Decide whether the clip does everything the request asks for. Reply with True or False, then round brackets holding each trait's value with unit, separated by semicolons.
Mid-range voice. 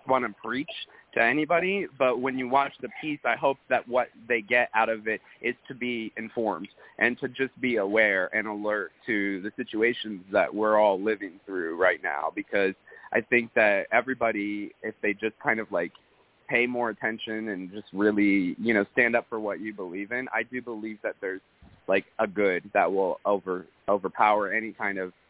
False (110 Hz)